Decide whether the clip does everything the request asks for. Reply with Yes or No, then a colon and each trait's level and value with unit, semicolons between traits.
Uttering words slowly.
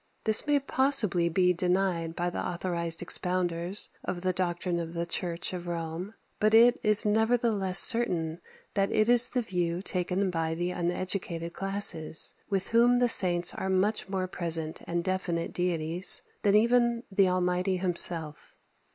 No: average, 150 wpm